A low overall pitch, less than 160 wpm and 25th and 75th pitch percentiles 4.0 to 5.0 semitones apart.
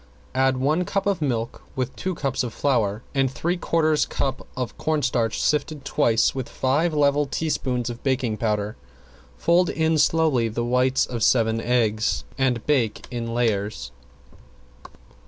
Yes: low, 130 Hz; average, 145 wpm; average, 4.3 semitones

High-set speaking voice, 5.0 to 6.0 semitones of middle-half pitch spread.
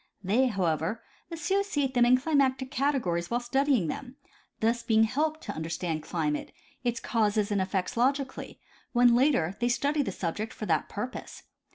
Yes: high, 240 Hz; wide, 5.6 semitones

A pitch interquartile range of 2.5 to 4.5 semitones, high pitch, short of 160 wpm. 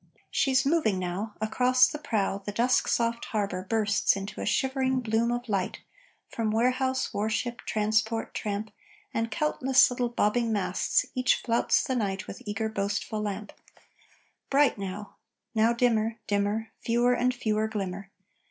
Yes: average, 3.1 semitones; high, 220 Hz; average, 145 wpm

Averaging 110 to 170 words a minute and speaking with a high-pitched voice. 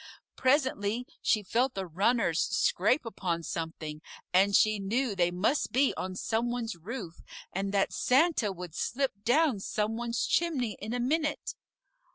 Yes: average, 150 wpm; high, 215 Hz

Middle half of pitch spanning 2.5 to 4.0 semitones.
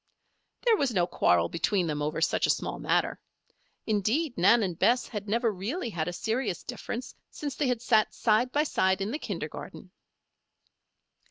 No: average, 5.2 semitones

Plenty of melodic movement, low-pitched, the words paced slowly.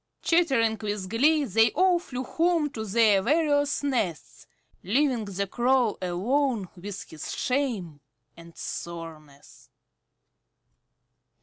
No: wide, 7.2 semitones; high, 230 Hz; slow, 105 wpm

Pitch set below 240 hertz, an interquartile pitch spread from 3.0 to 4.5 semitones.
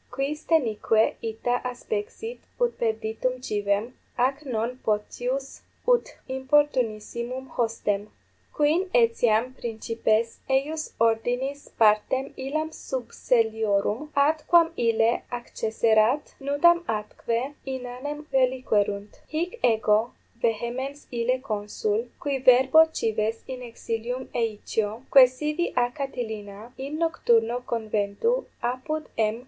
No: high, 245 Hz; average, 4.0 semitones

